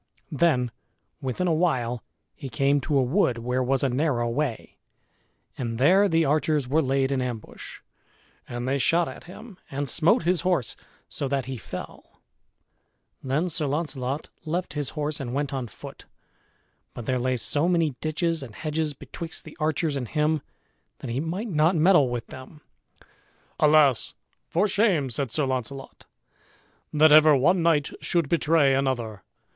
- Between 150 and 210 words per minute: Yes, average, 160 wpm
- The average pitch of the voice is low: No, medium, 145 Hz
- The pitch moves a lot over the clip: No, average, 3.8 semitones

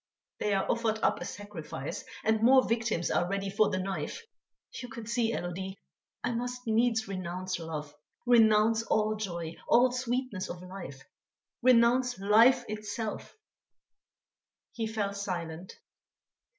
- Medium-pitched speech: No, high, 215 Hz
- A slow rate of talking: Yes, slow, 130 wpm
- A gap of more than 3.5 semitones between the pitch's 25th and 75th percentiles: Yes, average, 3.9 semitones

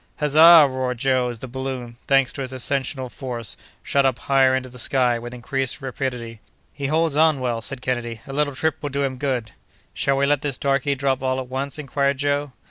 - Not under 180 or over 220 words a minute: Yes, average, 200 wpm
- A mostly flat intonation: Yes, narrow, 1.9 semitones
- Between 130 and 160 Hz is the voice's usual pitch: Yes, low, 135 Hz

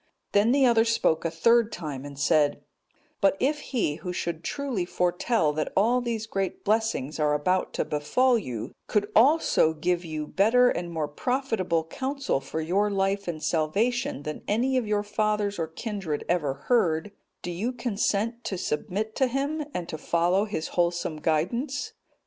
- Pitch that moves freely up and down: Yes, wide, 6.5 semitones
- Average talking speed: Yes, average, 165 wpm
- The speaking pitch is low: No, high, 195 Hz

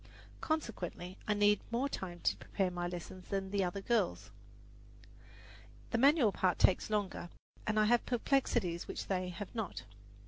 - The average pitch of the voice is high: Yes, high, 200 Hz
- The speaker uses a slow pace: No, average, 145 wpm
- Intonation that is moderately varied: Yes, average, 4.2 semitones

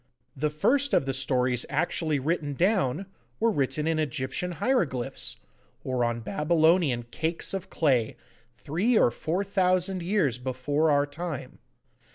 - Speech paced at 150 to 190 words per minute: No, slow, 135 wpm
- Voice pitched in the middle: Yes, medium, 155 Hz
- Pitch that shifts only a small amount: No, wide, 5.5 semitones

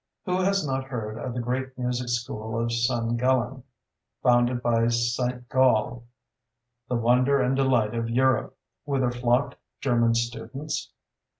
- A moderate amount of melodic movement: No, narrow, 2.0 semitones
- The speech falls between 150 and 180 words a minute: No, slow, 135 wpm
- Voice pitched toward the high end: No, low, 120 Hz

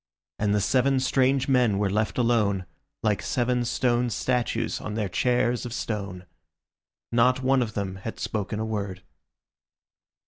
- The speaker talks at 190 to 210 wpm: No, average, 145 wpm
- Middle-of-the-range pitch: No, low, 115 Hz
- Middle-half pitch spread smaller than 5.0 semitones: Yes, average, 3.4 semitones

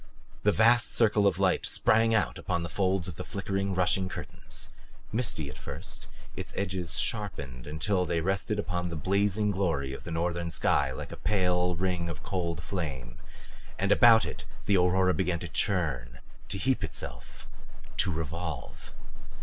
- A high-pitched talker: No, very low, 90 Hz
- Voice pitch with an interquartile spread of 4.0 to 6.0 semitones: No, average, 3.1 semitones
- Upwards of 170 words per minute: No, average, 160 wpm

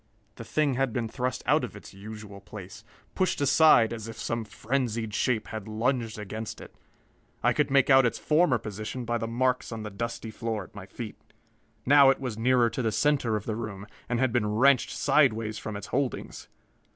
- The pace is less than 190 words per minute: No, average, 200 wpm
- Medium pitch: No, low, 115 Hz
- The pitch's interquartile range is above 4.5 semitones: No, average, 3.0 semitones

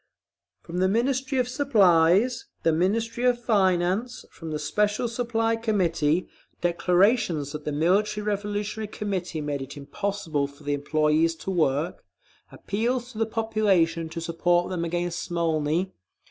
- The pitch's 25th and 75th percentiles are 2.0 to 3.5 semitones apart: No, average, 5.1 semitones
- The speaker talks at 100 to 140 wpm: Yes, slow, 135 wpm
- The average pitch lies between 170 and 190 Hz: Yes, medium, 185 Hz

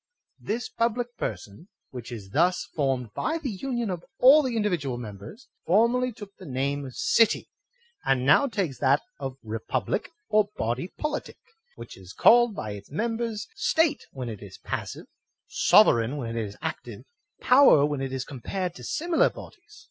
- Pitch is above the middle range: No, medium, 170 Hz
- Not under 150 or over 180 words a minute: Yes, average, 170 wpm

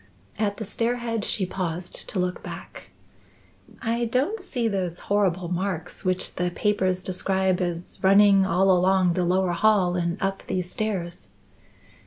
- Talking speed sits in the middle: Yes, average, 150 wpm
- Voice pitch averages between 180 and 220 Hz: Yes, high, 190 Hz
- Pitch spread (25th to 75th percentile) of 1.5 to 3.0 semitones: Yes, narrow, 2.6 semitones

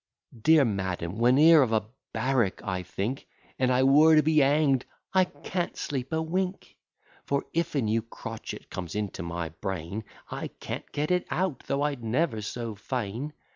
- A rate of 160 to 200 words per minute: Yes, average, 170 wpm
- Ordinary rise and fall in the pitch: No, wide, 6.4 semitones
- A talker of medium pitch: No, low, 130 Hz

